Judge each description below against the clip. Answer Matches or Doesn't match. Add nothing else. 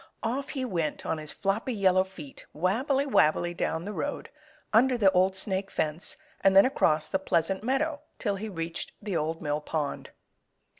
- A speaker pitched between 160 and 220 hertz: Matches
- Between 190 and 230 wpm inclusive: Doesn't match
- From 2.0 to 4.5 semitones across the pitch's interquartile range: Doesn't match